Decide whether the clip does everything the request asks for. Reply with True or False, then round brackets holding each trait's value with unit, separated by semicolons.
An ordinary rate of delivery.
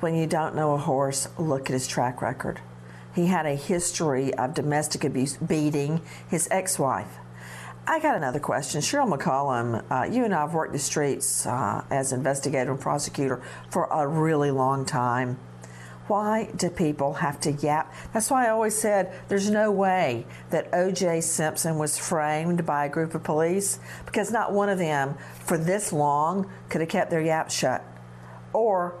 True (175 wpm)